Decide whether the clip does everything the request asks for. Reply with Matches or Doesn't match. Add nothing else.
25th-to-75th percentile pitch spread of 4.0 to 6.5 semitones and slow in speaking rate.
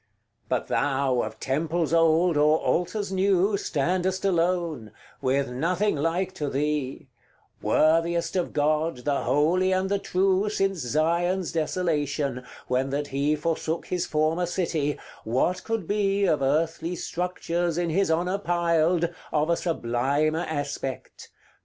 Doesn't match